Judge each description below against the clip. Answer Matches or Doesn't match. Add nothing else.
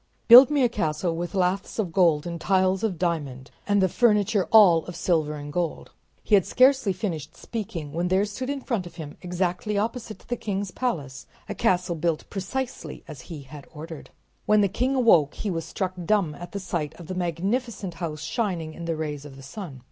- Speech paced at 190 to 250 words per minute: Matches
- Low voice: Doesn't match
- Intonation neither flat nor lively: Matches